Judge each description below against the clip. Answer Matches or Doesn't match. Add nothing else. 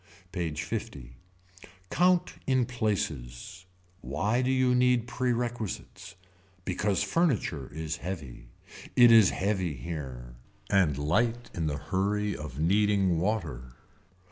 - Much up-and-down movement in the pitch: Matches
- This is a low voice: Matches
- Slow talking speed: Matches